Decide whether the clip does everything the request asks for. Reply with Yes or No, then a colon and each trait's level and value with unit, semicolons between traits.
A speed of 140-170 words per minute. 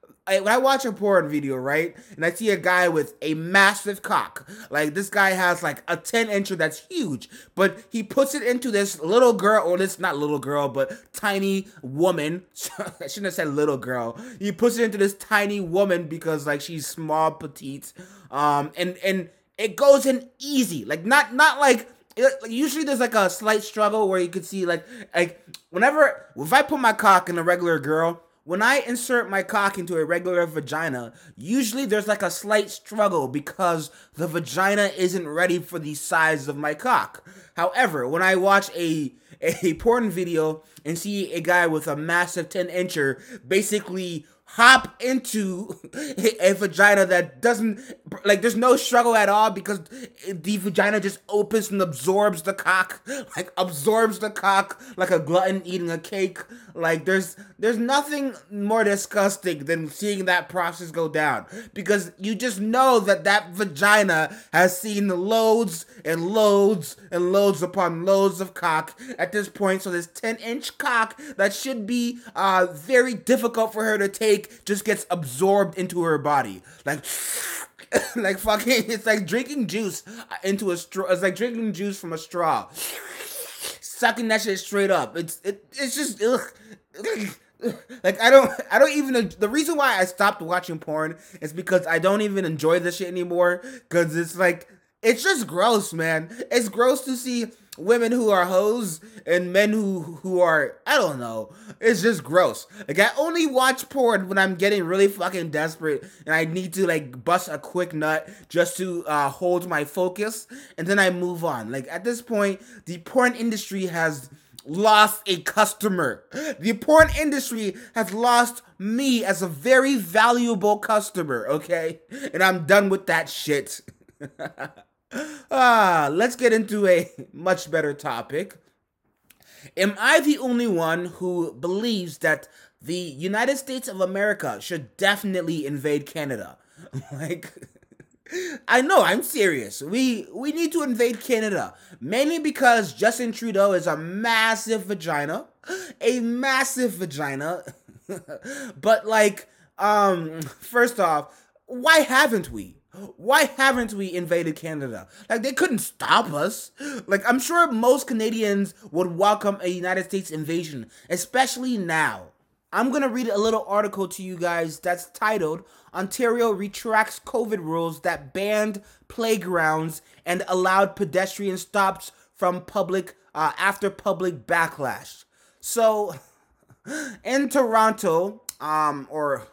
Yes: average, 160 wpm